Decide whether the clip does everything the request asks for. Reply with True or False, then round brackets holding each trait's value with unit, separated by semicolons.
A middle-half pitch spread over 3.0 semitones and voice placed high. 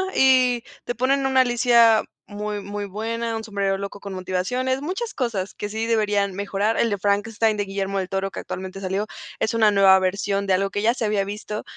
False (2.7 semitones; 205 Hz)